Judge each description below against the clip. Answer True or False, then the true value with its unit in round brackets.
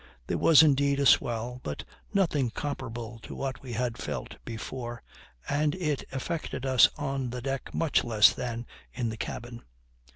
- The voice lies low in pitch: True (130 Hz)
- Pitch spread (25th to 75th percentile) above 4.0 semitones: False (3.0 semitones)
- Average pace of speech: True (160 wpm)